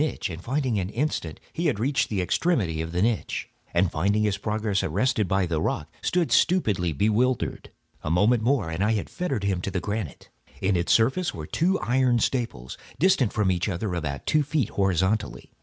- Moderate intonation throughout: No, wide, 6.2 semitones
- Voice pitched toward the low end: Yes, low, 105 Hz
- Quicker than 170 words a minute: Yes, average, 185 wpm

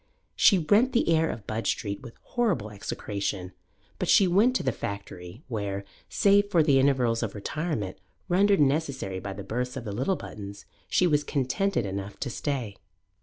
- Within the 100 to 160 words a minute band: No, average, 170 wpm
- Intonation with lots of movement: Yes, wide, 8.6 semitones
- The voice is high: No, low, 125 Hz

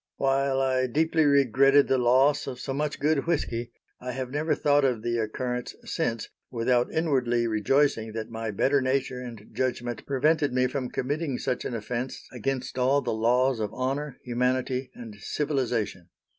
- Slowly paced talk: No, average, 160 wpm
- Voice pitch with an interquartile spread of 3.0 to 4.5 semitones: No, narrow, 2.5 semitones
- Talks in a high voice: No, low, 130 Hz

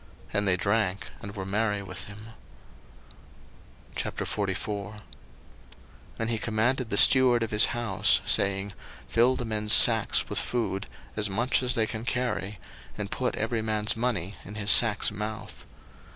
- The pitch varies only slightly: Yes, narrow, 2.3 semitones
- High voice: No, low, 110 Hz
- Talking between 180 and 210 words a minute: No, average, 145 wpm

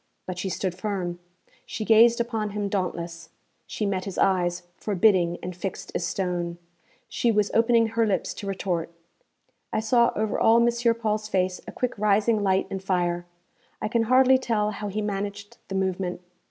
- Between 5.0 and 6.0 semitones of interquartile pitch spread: No, average, 3.3 semitones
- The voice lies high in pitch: Yes, high, 200 Hz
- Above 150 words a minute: Yes, average, 170 wpm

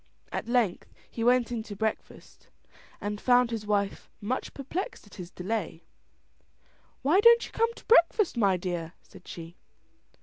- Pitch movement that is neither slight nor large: Yes, average, 4.9 semitones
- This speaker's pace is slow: No, average, 155 wpm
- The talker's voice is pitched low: No, high, 220 Hz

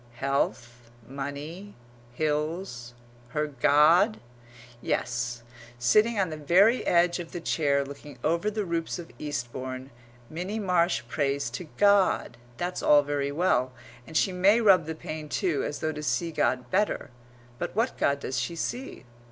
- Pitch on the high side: No, medium, 155 Hz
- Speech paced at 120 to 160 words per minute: Yes, average, 150 wpm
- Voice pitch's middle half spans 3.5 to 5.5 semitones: Yes, average, 4.7 semitones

